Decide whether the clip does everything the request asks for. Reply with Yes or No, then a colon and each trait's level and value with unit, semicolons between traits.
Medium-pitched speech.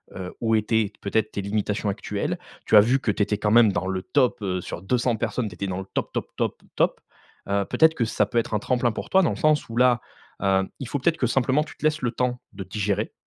No: low, 110 Hz